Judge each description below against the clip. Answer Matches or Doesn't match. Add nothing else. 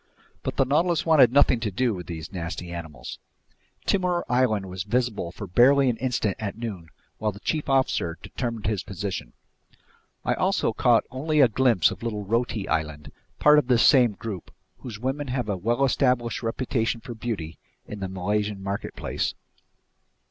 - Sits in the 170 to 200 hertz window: Doesn't match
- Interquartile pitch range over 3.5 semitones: Matches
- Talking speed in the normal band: Matches